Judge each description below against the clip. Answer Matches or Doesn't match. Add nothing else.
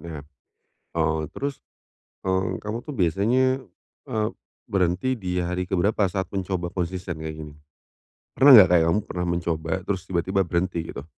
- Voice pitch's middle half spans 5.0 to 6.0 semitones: Doesn't match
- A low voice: Matches